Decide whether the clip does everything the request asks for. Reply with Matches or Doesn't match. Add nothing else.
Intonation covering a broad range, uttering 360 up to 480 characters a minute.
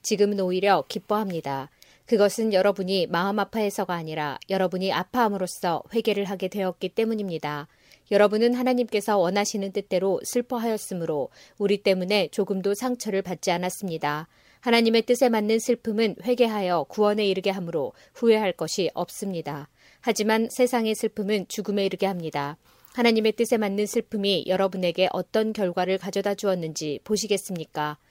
Doesn't match